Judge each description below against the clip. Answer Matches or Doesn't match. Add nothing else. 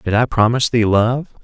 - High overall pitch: Doesn't match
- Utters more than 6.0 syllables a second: Doesn't match